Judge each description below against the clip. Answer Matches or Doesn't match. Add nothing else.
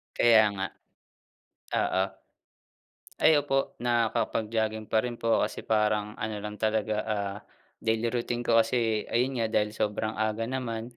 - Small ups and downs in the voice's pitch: Matches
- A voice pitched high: Doesn't match